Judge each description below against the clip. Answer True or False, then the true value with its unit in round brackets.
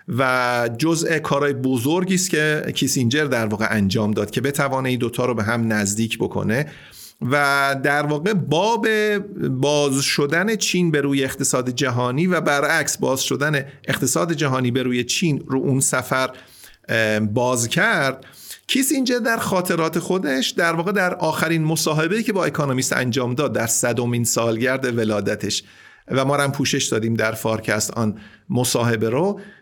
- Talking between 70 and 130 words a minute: False (150 wpm)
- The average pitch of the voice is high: False (135 Hz)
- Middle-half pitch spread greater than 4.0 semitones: True (5.0 semitones)